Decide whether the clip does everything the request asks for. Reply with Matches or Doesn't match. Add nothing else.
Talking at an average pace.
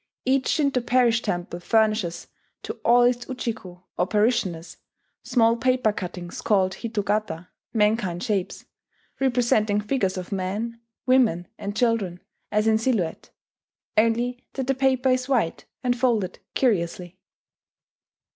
Doesn't match